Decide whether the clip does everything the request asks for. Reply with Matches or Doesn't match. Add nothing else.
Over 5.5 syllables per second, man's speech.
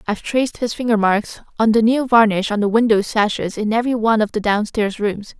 Doesn't match